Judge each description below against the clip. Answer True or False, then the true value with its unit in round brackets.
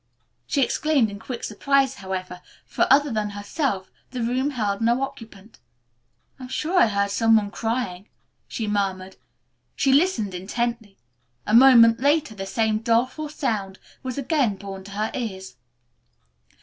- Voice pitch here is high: True (225 Hz)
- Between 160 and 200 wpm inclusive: False (145 wpm)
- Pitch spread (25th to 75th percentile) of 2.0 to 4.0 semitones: False (4.6 semitones)